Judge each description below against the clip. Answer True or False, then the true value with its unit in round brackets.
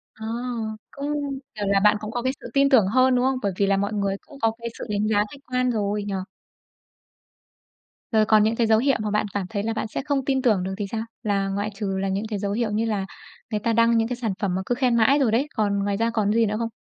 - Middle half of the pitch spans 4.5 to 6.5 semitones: False (2.8 semitones)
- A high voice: True (220 Hz)